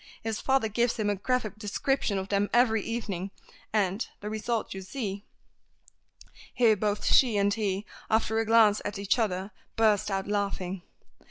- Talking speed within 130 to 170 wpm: Yes, average, 160 wpm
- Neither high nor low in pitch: No, high, 210 Hz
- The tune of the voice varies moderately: No, narrow, 2.2 semitones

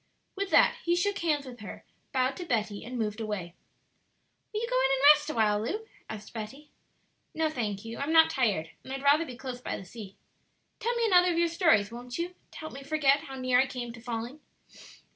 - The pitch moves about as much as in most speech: No, wide, 6.1 semitones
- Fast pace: Yes, fast, 220 wpm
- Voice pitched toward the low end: No, very high, 265 Hz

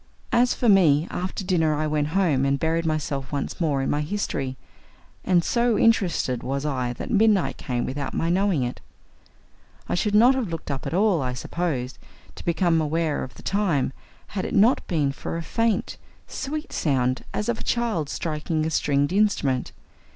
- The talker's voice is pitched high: No, medium, 160 Hz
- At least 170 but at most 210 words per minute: Yes, average, 180 wpm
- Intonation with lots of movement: Yes, wide, 6.0 semitones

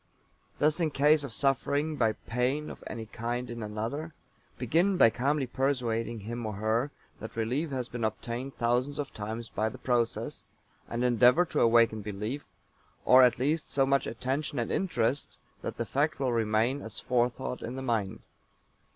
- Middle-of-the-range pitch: No, low, 125 Hz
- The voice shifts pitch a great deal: No, average, 3.6 semitones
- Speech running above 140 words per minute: Yes, average, 170 wpm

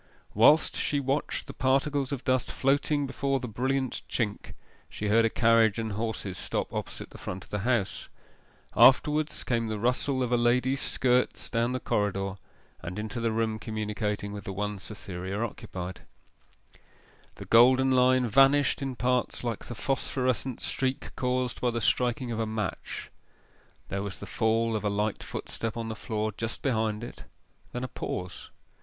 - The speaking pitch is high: No, low, 115 Hz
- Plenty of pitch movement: No, average, 3.3 semitones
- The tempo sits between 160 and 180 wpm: Yes, average, 165 wpm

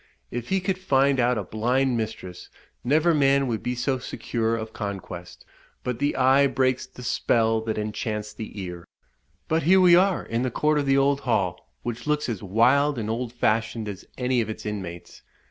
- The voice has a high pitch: No, low, 120 Hz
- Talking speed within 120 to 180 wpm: No, average, 190 wpm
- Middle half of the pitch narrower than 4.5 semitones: Yes, average, 4.1 semitones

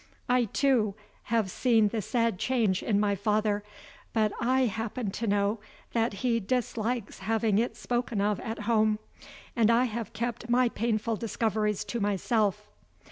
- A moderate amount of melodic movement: No, narrow, 2.2 semitones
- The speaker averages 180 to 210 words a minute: No, average, 150 wpm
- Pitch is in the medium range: No, high, 220 Hz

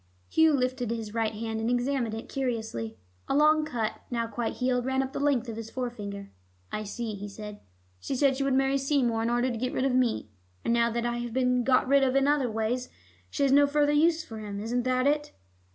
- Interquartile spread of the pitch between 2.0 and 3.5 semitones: Yes, average, 3.2 semitones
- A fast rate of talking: Yes, fast, 230 wpm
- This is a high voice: Yes, high, 245 Hz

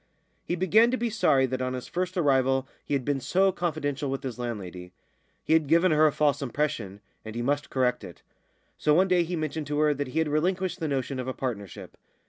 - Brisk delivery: Yes, fast, 225 wpm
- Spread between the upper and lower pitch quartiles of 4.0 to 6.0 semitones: Yes, average, 4.5 semitones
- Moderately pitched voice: Yes, medium, 145 Hz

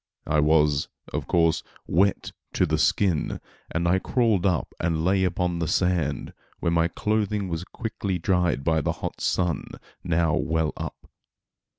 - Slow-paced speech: No, average, 155 wpm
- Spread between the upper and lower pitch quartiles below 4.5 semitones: Yes, average, 2.8 semitones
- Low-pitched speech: Yes, very low, 85 Hz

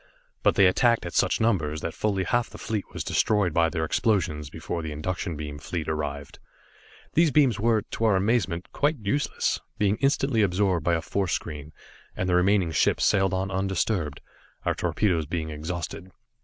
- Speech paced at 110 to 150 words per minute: No, average, 175 wpm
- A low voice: Yes, very low, 95 Hz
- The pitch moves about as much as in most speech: Yes, average, 4.9 semitones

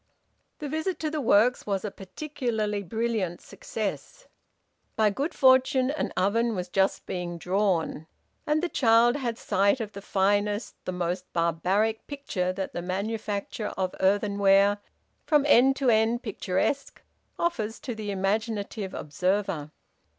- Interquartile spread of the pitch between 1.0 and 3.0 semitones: No, average, 4.5 semitones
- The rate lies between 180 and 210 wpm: No, slow, 135 wpm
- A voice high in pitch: Yes, high, 210 Hz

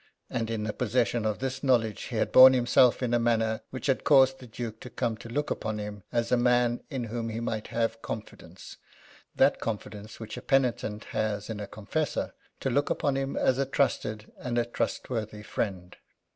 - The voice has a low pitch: Yes, low, 115 Hz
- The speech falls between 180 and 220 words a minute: Yes, average, 200 wpm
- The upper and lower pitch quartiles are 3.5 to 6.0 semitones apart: No, average, 2.8 semitones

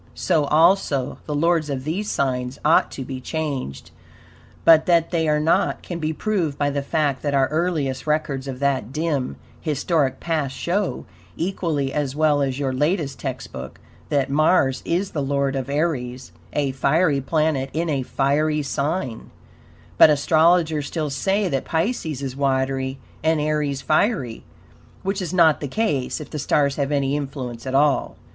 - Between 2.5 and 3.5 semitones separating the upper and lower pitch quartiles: Yes, average, 3.0 semitones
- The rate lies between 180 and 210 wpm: No, average, 165 wpm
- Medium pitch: Yes, medium, 145 Hz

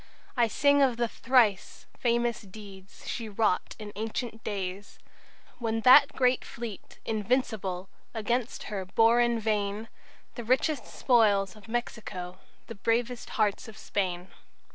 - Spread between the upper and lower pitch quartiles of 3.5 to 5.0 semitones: No, average, 3.0 semitones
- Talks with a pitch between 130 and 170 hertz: No, high, 225 Hz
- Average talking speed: No, slow, 130 wpm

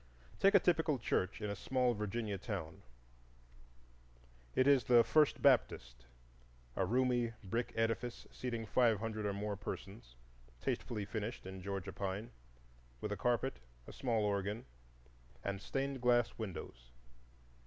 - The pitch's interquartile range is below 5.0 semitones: Yes, average, 4.0 semitones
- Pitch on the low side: Yes, low, 110 Hz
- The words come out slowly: Yes, slow, 130 wpm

